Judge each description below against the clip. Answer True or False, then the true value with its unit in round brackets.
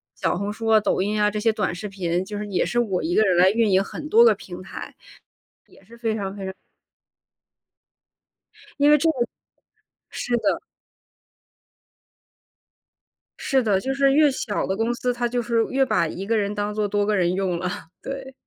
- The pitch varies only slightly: False (3.6 semitones)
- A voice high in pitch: True (215 Hz)